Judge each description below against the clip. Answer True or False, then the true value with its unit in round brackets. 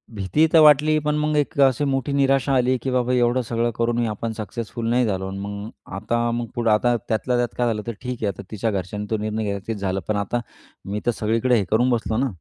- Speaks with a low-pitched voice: True (120 Hz)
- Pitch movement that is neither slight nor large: True (3.2 semitones)